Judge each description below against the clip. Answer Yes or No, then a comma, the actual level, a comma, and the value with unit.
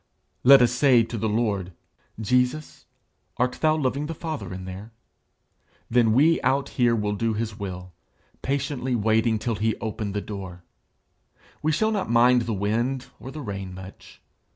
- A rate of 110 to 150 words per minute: No, average, 160 wpm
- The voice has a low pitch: Yes, low, 115 Hz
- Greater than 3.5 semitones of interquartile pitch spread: Yes, average, 4.2 semitones